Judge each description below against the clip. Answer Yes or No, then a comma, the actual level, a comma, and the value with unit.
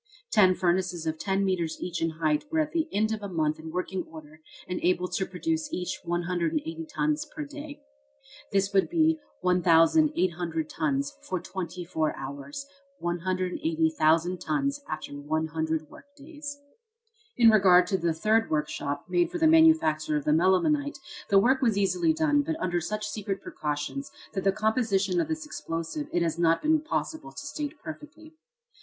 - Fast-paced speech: No, average, 165 wpm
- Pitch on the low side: No, high, 190 Hz